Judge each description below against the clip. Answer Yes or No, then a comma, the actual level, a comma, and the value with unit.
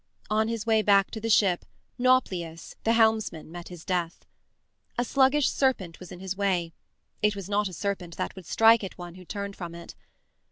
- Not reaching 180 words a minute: No, average, 195 wpm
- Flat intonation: No, average, 4.0 semitones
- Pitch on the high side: Yes, high, 200 Hz